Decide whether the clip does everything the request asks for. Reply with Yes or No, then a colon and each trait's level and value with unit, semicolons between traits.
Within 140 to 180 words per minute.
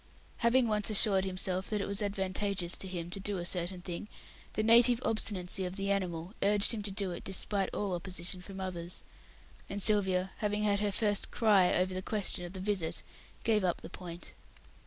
No: average, 195 wpm